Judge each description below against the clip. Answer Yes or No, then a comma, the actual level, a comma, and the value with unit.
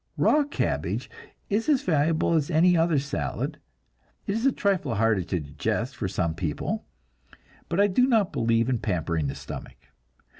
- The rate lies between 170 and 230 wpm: No, average, 160 wpm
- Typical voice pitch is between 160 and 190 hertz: No, medium, 145 Hz